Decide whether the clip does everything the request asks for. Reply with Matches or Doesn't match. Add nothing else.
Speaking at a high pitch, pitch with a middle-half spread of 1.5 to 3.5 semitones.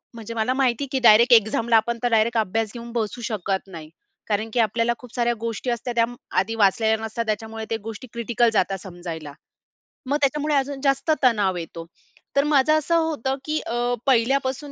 Matches